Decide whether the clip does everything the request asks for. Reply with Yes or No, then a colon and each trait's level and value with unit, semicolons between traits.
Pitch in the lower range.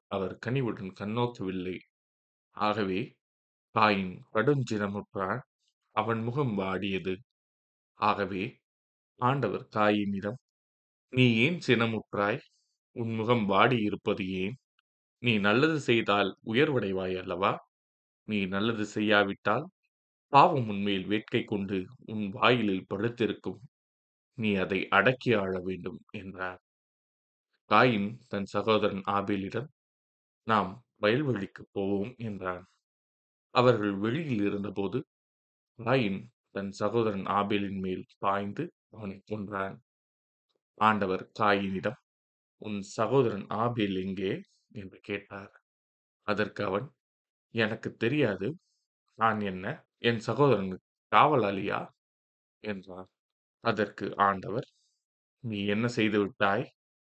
Yes: low, 100 Hz